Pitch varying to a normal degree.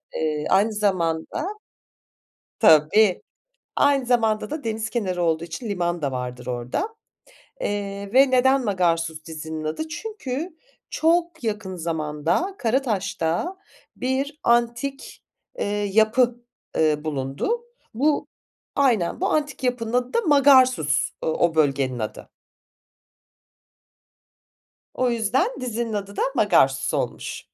No: wide, 8.3 semitones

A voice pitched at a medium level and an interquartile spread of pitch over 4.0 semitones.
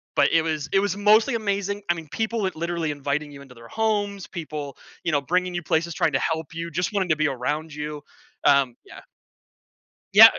Yes: medium, 165 Hz; average, 5.1 semitones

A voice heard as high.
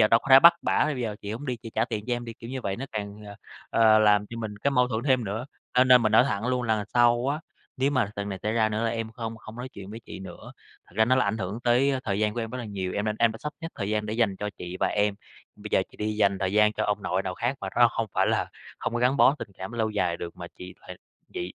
No: low, 110 Hz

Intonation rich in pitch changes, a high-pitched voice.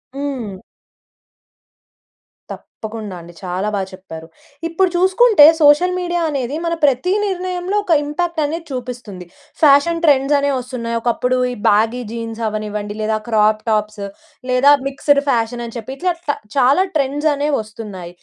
Yes: wide, 5.7 semitones; very high, 255 Hz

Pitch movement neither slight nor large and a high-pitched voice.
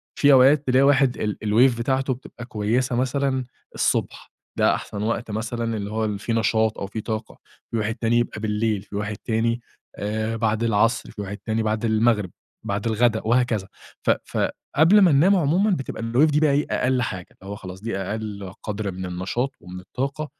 No: average, 3.5 semitones; low, 115 Hz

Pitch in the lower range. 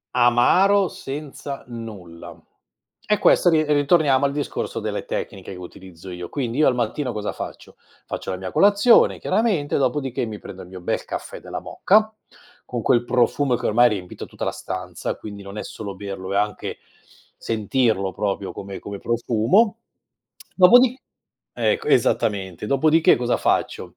Yes: low, 120 Hz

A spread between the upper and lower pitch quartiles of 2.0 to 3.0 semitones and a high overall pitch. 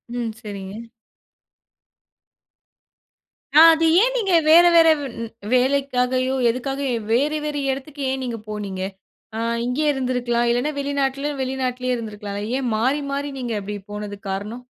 No: average, 3.5 semitones; very high, 255 Hz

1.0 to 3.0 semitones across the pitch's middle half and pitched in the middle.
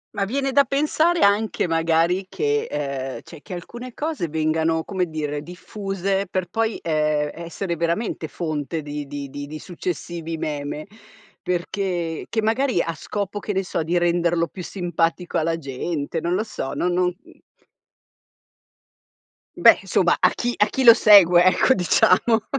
No: average, 4.2 semitones; medium, 175 Hz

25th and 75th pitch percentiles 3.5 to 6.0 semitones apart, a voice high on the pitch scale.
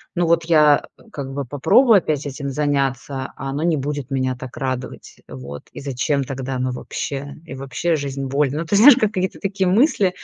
No: average, 4.0 semitones; medium, 140 Hz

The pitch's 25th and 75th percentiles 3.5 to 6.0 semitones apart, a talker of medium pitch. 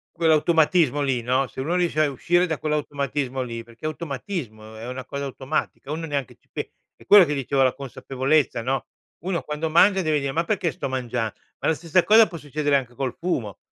Yes: average, 4.0 semitones; medium, 145 Hz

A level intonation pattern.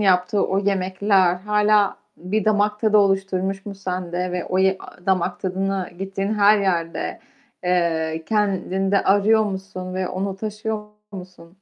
Yes: narrow, 1.9 semitones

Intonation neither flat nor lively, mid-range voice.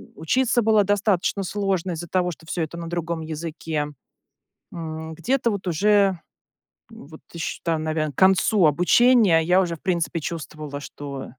Yes: average, 3.7 semitones; medium, 170 Hz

